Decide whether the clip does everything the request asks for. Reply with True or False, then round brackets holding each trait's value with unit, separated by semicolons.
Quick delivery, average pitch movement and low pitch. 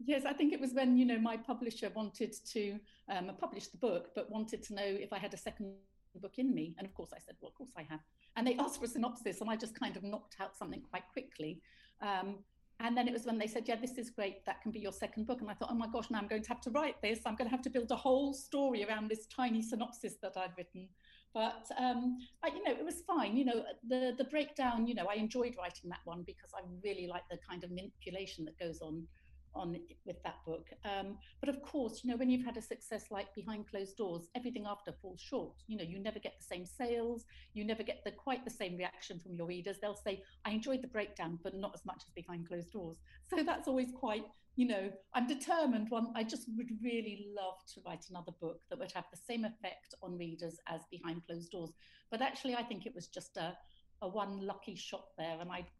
False (250 wpm; 4.5 semitones; 215 Hz)